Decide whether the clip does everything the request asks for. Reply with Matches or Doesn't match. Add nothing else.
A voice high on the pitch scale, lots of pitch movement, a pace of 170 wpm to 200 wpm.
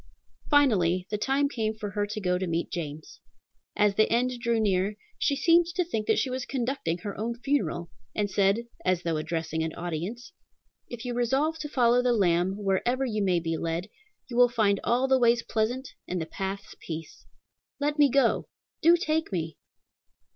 Matches